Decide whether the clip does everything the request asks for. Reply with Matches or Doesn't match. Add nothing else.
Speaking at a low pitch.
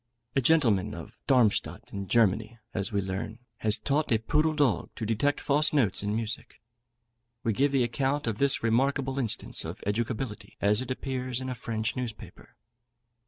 Matches